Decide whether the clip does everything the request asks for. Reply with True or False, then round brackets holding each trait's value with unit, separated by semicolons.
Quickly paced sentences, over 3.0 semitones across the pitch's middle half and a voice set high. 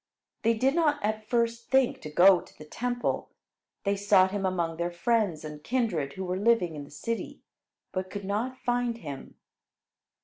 False (175 wpm; 5.3 semitones; 200 Hz)